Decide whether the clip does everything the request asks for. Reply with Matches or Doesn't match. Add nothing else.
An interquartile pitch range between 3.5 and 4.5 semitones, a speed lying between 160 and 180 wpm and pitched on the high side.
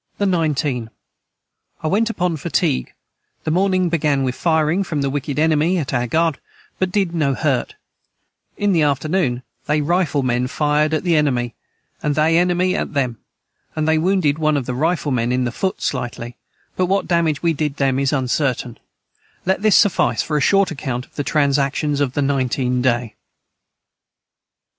Doesn't match